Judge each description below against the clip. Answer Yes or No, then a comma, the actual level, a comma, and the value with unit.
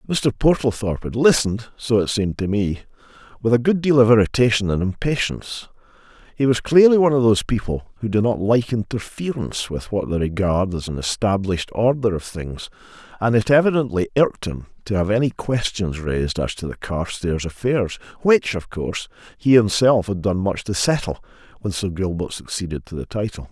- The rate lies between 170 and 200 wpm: Yes, average, 175 wpm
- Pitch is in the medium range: No, low, 105 Hz